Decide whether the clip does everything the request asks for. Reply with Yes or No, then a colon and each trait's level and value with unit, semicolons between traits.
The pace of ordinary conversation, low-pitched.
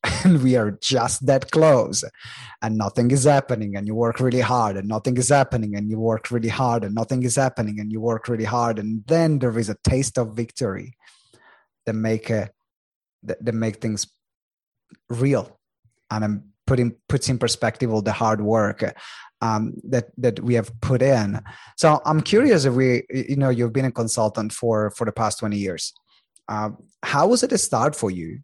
Yes: average, 190 wpm; low, 115 Hz